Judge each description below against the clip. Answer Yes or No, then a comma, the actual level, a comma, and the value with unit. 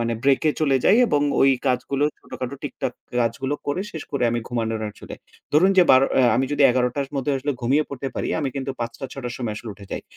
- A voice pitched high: No, low, 135 Hz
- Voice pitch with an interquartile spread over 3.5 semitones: No, average, 2.8 semitones